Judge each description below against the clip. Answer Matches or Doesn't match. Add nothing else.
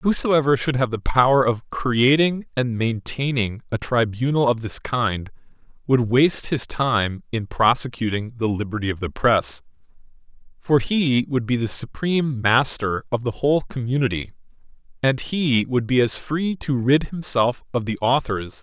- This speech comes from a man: Matches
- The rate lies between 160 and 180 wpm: Matches